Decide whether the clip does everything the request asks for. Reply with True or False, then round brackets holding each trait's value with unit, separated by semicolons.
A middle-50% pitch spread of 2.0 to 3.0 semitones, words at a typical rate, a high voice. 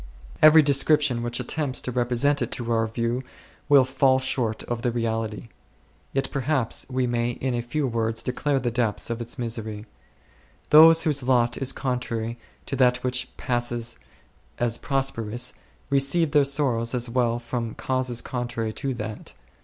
False (2.5 semitones; 160 wpm; 125 Hz)